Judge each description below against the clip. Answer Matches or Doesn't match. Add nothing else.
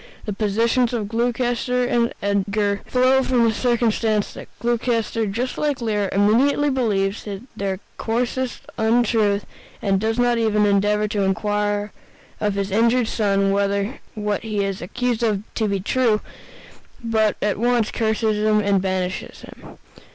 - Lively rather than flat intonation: Doesn't match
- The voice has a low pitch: Doesn't match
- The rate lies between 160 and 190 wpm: Doesn't match